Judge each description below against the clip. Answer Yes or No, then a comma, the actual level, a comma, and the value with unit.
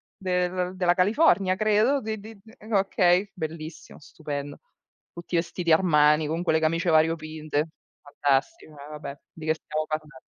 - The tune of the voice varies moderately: Yes, average, 3.4 semitones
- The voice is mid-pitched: Yes, medium, 165 Hz